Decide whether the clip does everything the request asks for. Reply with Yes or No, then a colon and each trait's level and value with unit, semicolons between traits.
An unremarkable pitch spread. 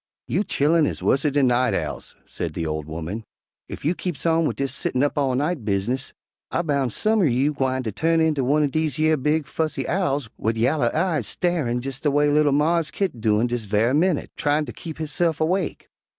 Yes: average, 4.2 semitones